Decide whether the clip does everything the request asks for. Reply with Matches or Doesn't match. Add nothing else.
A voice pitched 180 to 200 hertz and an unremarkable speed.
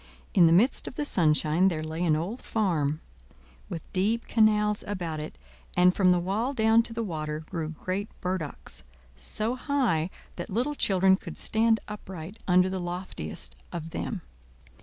Matches